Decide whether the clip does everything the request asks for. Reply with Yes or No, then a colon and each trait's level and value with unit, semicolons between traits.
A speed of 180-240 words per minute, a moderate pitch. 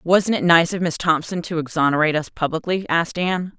Yes: average, 200 wpm; medium, 170 Hz